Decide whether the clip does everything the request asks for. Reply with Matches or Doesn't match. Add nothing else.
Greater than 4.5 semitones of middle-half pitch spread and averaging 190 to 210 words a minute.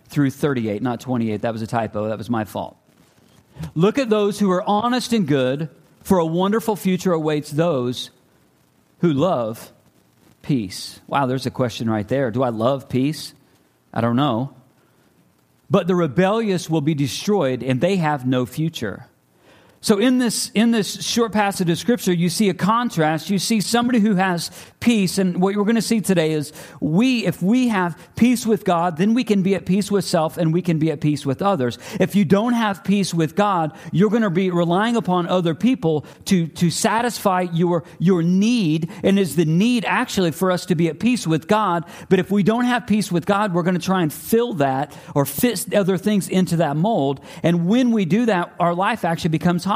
Matches